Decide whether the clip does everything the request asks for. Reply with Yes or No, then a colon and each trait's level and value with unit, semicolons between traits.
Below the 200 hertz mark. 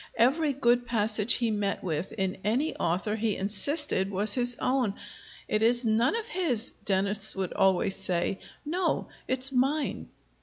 No: high, 220 Hz